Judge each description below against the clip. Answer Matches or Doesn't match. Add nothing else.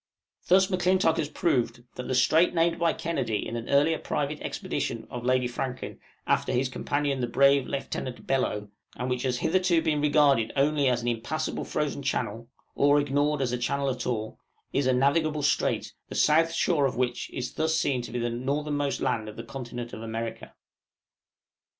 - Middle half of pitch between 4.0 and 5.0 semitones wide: Doesn't match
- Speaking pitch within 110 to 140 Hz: Matches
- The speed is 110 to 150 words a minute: Doesn't match